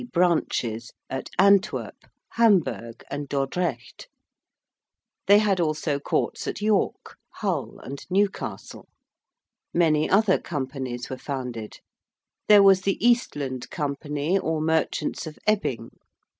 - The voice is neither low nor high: Yes, medium, 155 Hz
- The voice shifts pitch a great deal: Yes, wide, 6.2 semitones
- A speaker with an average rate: No, slow, 105 wpm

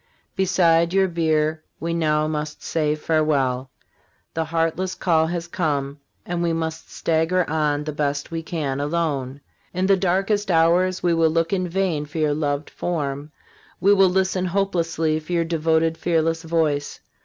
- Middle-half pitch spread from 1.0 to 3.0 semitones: Yes, narrow, 2.4 semitones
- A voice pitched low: No, medium, 165 Hz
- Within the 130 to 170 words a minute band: Yes, average, 155 wpm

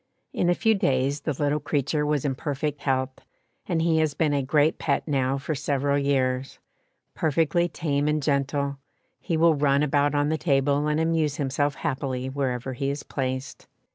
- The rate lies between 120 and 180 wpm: Yes, average, 175 wpm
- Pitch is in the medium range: Yes, medium, 145 Hz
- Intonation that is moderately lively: No, narrow, 2.0 semitones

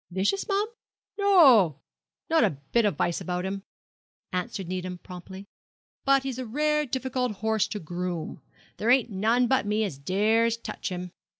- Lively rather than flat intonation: Yes, wide, 5.9 semitones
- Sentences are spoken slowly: No, average, 160 wpm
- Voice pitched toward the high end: Yes, high, 215 Hz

